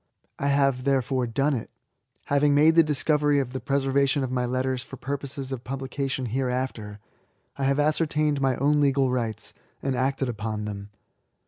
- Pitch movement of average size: No, narrow, 1.9 semitones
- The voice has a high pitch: No, low, 135 Hz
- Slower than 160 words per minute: No, average, 165 wpm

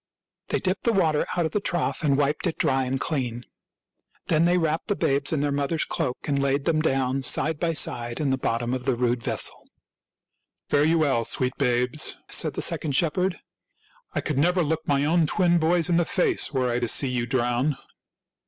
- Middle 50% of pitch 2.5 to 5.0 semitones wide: Yes, average, 4.2 semitones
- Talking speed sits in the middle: No, fast, 210 wpm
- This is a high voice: No, medium, 145 Hz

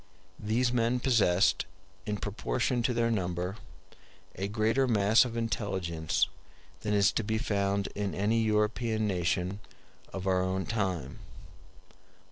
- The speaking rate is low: Yes, slow, 125 wpm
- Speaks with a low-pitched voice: Yes, low, 105 Hz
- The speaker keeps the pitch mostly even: No, average, 3.3 semitones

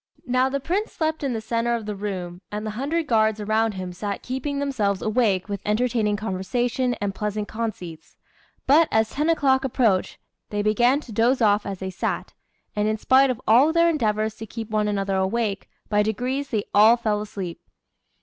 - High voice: Yes, high, 220 Hz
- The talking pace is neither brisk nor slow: Yes, average, 190 wpm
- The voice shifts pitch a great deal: No, average, 3.6 semitones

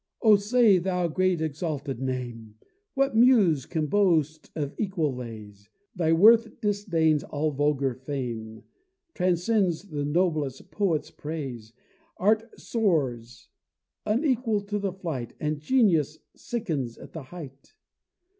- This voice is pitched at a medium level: Yes, medium, 160 Hz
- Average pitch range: No, wide, 6.8 semitones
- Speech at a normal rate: No, slow, 115 wpm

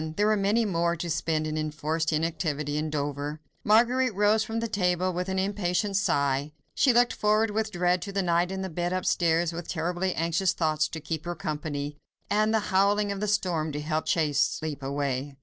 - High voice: No, medium, 175 Hz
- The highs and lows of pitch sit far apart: No, average, 4.5 semitones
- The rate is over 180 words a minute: Yes, average, 200 wpm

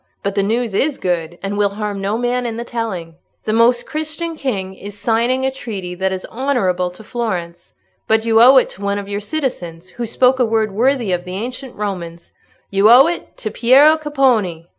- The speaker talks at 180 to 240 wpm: Yes, average, 200 wpm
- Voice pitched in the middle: No, high, 220 Hz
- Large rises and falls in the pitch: No, average, 4.7 semitones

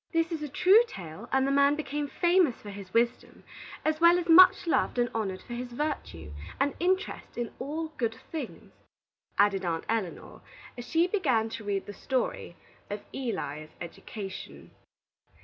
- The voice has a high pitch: Yes, very high, 250 Hz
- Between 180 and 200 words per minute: No, average, 165 wpm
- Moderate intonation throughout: No, wide, 7.8 semitones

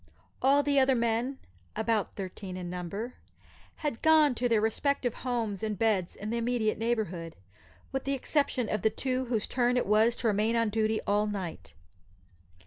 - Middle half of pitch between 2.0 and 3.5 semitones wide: Yes, average, 3.2 semitones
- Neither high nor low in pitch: No, high, 225 Hz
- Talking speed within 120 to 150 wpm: No, average, 170 wpm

